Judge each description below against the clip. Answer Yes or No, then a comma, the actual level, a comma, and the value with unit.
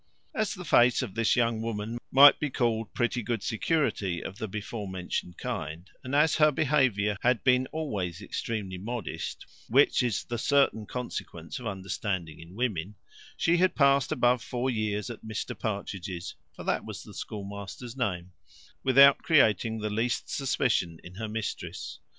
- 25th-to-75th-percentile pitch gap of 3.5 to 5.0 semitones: Yes, average, 4.3 semitones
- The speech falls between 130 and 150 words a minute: No, average, 160 wpm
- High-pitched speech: No, low, 115 Hz